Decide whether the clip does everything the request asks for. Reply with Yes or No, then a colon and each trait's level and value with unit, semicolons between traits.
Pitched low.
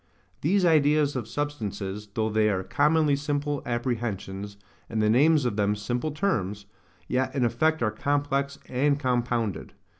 Yes: low, 125 Hz